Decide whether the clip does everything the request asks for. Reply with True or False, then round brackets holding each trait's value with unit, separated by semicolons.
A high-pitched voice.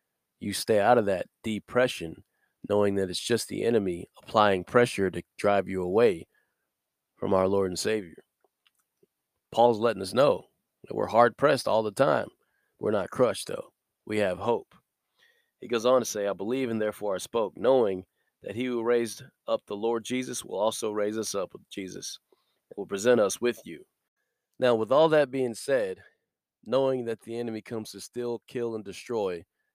False (115 Hz)